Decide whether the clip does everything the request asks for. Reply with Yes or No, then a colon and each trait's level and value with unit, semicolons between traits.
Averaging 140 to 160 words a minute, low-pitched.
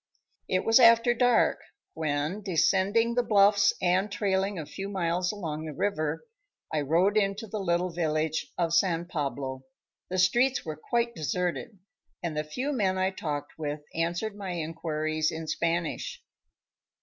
No: average, 150 wpm; medium, 180 Hz